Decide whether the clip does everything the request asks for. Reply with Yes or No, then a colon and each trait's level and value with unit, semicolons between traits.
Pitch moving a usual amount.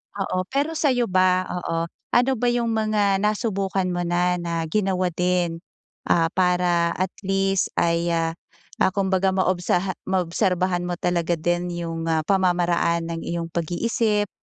No: narrow, 2.2 semitones